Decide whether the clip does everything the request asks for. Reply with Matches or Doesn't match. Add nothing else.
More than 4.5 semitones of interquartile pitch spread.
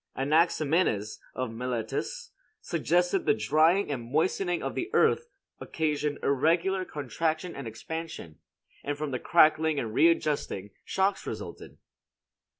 Matches